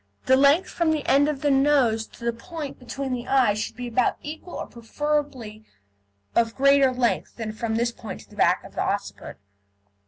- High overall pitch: Yes, very high, 260 Hz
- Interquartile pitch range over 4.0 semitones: No, average, 3.7 semitones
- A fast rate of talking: No, average, 195 wpm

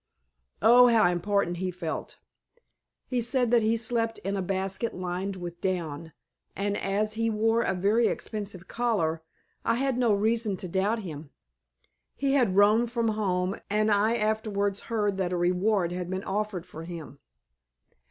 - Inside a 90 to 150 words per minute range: No, average, 160 wpm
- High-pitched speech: Yes, high, 205 Hz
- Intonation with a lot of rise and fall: No, average, 3.7 semitones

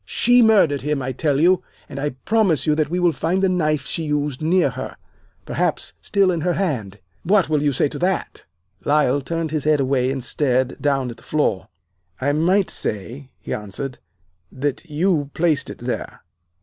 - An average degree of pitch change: Yes, average, 4.3 semitones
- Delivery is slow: No, average, 190 wpm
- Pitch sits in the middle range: Yes, medium, 150 Hz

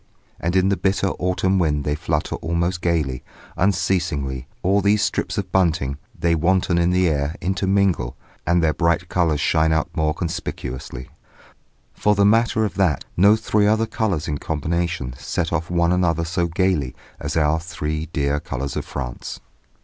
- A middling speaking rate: Yes, average, 165 wpm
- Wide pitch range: No, average, 3.6 semitones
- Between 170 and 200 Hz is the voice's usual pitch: No, very low, 85 Hz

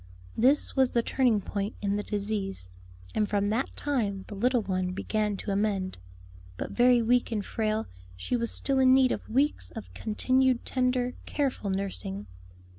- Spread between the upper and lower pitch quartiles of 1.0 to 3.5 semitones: No, average, 4.1 semitones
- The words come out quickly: No, average, 165 wpm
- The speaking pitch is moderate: No, high, 215 Hz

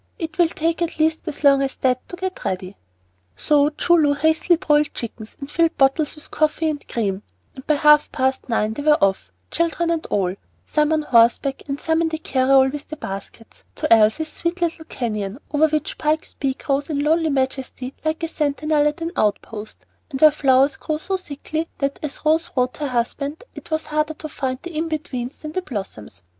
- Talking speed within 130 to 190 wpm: No, average, 200 wpm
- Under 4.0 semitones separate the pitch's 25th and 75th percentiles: Yes, average, 3.4 semitones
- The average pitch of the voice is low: No, very high, 295 Hz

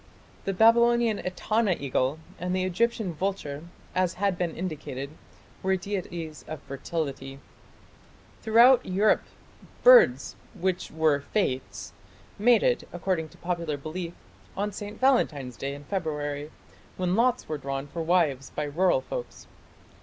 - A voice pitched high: No, medium, 180 Hz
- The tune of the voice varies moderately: No, wide, 5.7 semitones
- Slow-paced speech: Yes, slow, 125 wpm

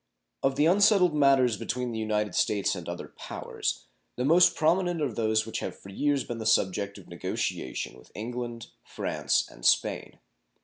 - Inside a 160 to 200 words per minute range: Yes, average, 170 wpm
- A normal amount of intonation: No, wide, 5.7 semitones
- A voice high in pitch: No, low, 120 Hz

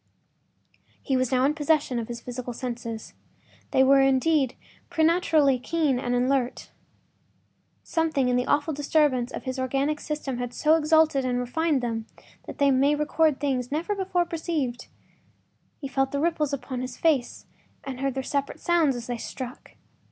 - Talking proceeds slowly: No, average, 165 wpm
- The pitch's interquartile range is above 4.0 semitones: No, average, 3.5 semitones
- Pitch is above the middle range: Yes, very high, 275 Hz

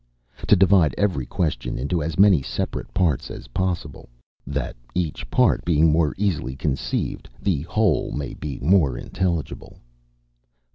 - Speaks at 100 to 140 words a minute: Yes, slow, 135 wpm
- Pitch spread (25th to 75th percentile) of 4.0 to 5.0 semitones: Yes, average, 4.6 semitones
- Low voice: Yes, very low, 80 Hz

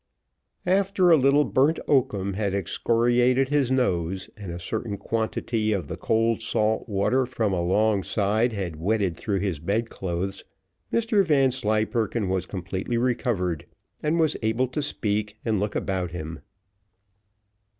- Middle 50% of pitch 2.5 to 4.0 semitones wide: No, average, 4.7 semitones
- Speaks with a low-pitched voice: Yes, low, 110 Hz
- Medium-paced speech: No, slow, 130 wpm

